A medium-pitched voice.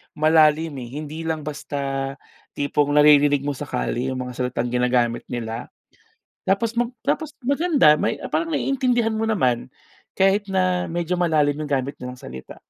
Yes: medium, 150 Hz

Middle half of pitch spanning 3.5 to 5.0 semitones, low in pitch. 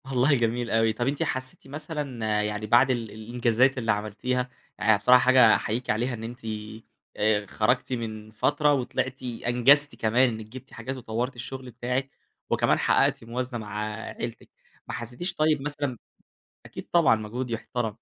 No: average, 2.8 semitones; low, 120 Hz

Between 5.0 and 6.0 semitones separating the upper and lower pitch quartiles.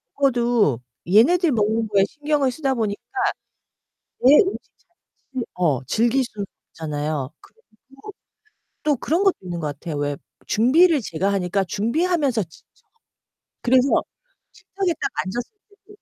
No: wide, 8.1 semitones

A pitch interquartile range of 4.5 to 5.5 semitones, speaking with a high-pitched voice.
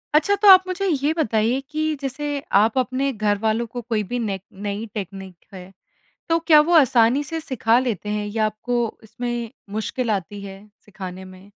Yes: average, 4.8 semitones; high, 230 Hz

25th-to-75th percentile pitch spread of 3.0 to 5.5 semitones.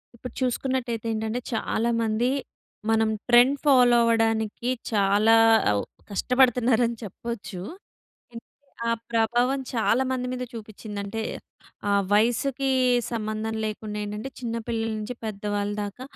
No: narrow, 2.4 semitones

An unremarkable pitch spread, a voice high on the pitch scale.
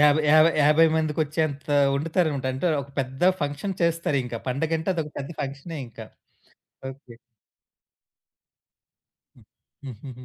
No: average, 3.0 semitones; medium, 145 Hz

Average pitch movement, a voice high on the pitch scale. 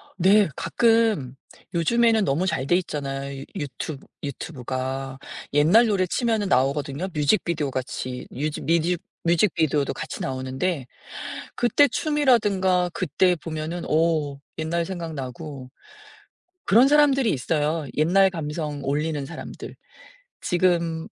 No: average, 5.0 semitones; medium, 160 Hz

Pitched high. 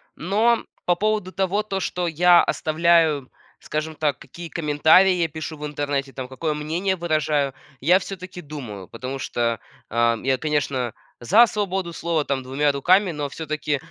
No: medium, 155 Hz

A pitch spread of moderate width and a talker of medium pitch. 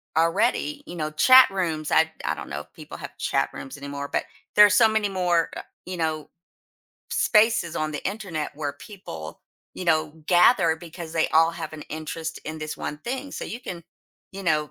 Yes: average, 3.7 semitones; medium, 165 Hz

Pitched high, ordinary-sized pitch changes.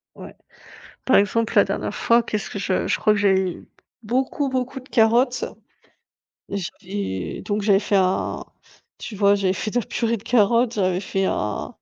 Yes: high, 210 Hz; average, 3.2 semitones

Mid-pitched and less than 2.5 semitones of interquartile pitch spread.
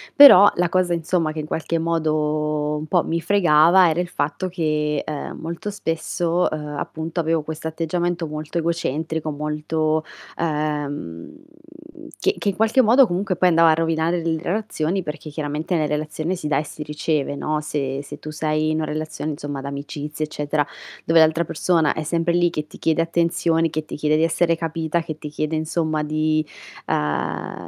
Yes: medium, 160 Hz; narrow, 1.8 semitones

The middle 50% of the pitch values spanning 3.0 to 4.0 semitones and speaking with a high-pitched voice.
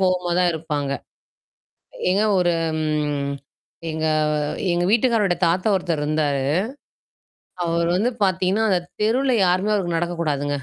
No: average, 3.6 semitones; medium, 175 Hz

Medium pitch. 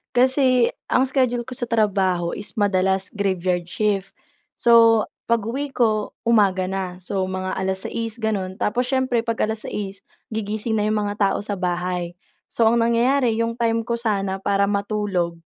No: high, 210 Hz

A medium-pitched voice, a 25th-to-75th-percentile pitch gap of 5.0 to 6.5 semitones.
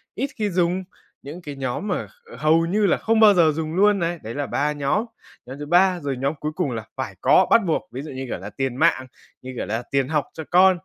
Yes: medium, 160 Hz; average, 5.3 semitones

